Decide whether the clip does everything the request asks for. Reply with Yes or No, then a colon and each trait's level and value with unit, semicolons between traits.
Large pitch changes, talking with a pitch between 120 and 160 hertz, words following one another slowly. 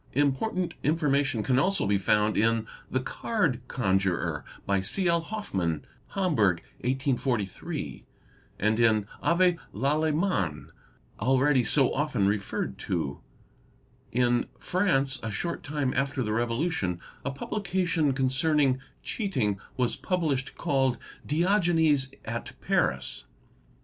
Yes: wide, 6.7 semitones; low, 135 Hz; slow, 115 wpm